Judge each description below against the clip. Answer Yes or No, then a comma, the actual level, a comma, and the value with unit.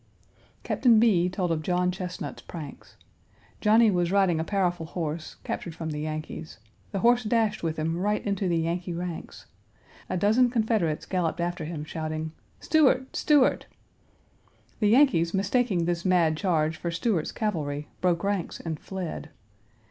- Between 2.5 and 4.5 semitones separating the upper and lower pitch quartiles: Yes, average, 4.1 semitones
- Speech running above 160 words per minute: No, average, 150 wpm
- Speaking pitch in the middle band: Yes, medium, 175 Hz